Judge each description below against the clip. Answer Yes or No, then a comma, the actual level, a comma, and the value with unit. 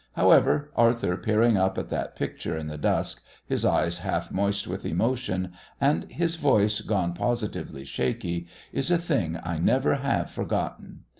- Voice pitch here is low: Yes, low, 105 Hz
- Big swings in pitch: Yes, wide, 6.9 semitones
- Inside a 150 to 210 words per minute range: Yes, average, 155 wpm